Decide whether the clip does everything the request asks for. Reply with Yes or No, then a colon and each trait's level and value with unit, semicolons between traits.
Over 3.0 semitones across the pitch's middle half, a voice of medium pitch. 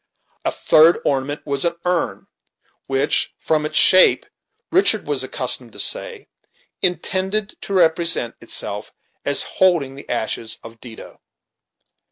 Yes: wide, 5.5 semitones; medium, 160 Hz